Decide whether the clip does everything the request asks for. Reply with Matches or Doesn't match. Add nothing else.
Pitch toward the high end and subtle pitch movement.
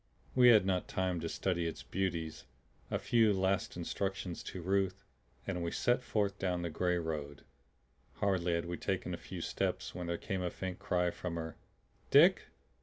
Doesn't match